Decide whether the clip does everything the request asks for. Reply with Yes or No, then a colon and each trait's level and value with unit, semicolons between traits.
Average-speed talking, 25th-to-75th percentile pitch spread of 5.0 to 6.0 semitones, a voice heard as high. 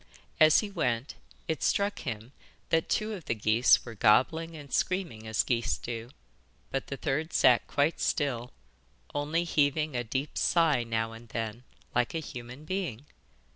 No: average, 160 wpm; wide, 5.5 semitones; low, 135 Hz